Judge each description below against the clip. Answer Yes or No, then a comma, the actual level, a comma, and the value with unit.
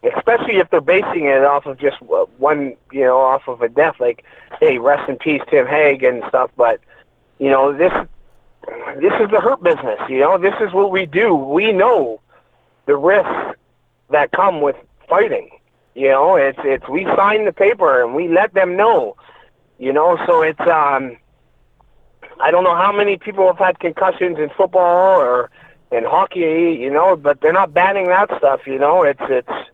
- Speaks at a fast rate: No, average, 185 wpm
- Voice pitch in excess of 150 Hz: Yes, high, 190 Hz